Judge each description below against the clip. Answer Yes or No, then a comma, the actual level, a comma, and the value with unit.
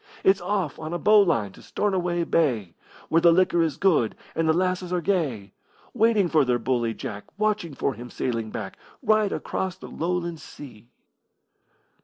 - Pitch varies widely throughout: Yes, wide, 7.0 semitones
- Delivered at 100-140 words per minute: No, average, 165 wpm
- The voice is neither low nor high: Yes, medium, 170 Hz